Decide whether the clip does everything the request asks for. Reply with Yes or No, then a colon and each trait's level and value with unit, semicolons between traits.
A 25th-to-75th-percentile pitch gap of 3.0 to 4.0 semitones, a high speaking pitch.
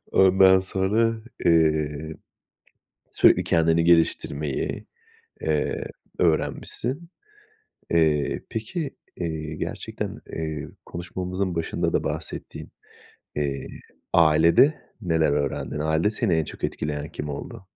No: average, 3.6 semitones; very low, 80 Hz